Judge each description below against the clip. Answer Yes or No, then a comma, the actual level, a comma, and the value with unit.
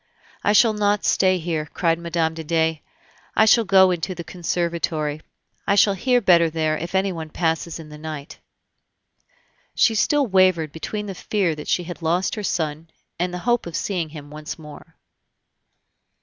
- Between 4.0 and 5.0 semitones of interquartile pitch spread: No, average, 3.3 semitones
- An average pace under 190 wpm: Yes, average, 170 wpm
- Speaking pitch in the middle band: Yes, medium, 170 Hz